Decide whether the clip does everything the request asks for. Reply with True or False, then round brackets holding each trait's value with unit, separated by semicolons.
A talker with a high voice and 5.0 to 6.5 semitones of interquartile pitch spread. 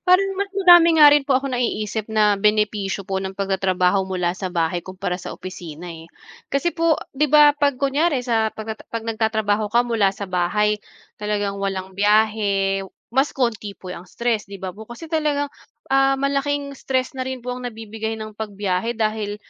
True (220 Hz; 5.3 semitones)